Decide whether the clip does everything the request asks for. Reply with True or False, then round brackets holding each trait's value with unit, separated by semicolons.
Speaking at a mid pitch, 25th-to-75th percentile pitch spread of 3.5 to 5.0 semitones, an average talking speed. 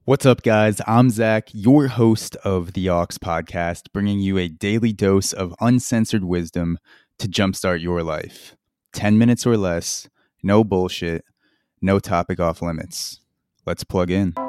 False (95 Hz; 4.3 semitones; 150 wpm)